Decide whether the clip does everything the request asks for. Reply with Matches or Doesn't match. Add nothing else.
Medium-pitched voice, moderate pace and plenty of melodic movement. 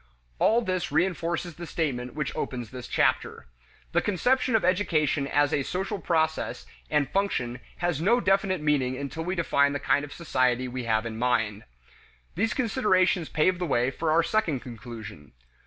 Matches